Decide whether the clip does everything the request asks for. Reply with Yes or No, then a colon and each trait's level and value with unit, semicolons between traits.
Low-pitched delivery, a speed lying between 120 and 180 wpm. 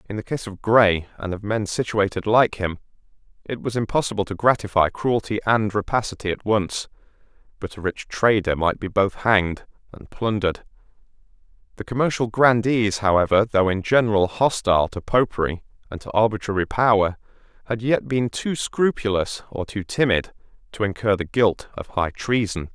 Yes: low, 105 Hz; average, 160 wpm